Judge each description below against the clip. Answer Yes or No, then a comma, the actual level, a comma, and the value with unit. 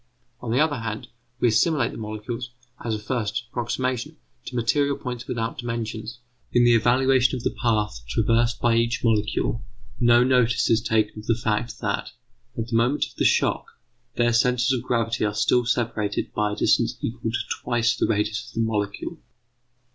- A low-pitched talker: Yes, low, 115 Hz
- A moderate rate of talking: Yes, average, 180 wpm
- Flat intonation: Yes, narrow, 1.9 semitones